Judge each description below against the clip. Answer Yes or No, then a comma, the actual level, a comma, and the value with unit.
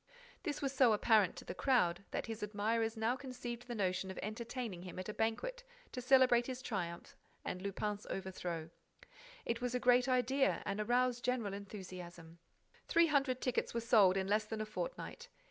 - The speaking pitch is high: Yes, high, 225 Hz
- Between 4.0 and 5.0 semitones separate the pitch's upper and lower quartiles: Yes, average, 4.3 semitones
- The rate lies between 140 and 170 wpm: No, average, 180 wpm